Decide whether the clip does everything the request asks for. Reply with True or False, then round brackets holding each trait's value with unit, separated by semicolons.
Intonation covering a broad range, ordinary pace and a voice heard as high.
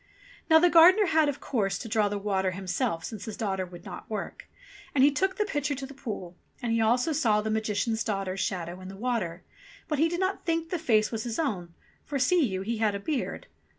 False (7.0 semitones; 230 wpm; 225 Hz)